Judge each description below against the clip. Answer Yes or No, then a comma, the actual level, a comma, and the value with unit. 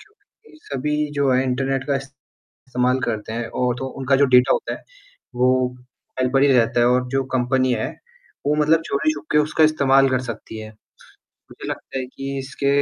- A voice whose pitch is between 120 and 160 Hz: Yes, low, 135 Hz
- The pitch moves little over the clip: Yes, narrow, 2.0 semitones